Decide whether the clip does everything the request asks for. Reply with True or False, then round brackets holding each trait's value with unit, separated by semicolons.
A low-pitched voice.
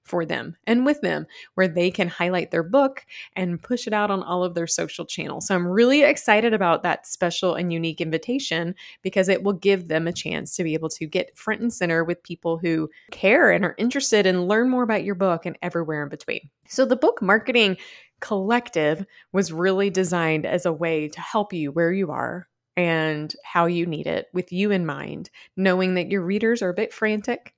False (180 Hz)